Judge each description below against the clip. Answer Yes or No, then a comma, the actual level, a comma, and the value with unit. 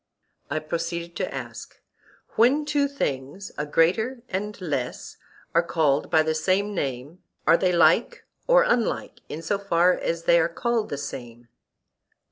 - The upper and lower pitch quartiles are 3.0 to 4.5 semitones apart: No, average, 5.2 semitones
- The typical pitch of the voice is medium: Yes, medium, 170 Hz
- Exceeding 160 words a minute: No, average, 150 wpm